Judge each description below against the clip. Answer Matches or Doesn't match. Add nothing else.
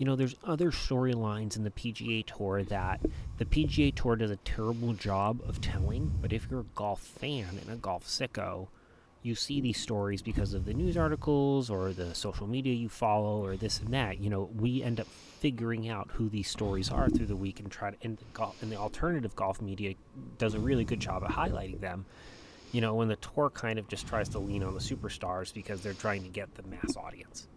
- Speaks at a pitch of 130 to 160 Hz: Doesn't match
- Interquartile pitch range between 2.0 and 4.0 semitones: Matches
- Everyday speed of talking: Doesn't match